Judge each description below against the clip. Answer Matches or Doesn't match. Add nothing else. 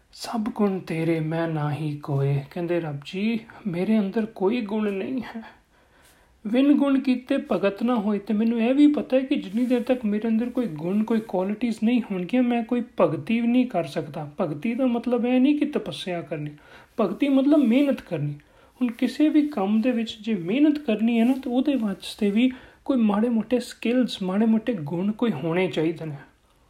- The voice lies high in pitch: Matches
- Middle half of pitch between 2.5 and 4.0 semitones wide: Doesn't match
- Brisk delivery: Matches